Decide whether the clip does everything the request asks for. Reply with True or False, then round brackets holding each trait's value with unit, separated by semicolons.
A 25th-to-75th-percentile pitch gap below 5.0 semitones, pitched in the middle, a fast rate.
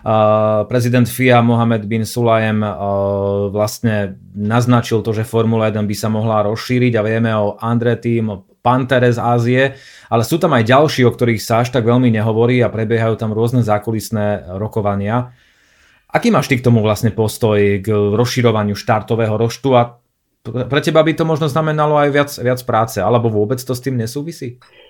False (2.5 semitones; 115 Hz; 175 wpm)